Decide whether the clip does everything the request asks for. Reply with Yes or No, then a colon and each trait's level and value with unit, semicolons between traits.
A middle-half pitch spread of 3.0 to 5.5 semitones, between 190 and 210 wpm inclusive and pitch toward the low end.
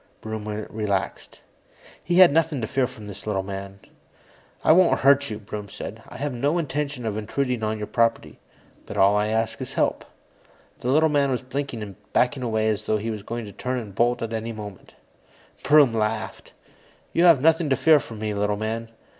Yes: average, 4.7 semitones; average, 195 wpm; low, 115 Hz